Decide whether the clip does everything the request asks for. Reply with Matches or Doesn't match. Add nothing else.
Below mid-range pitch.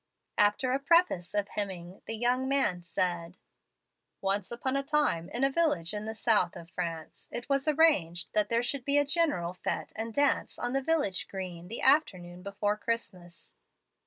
Doesn't match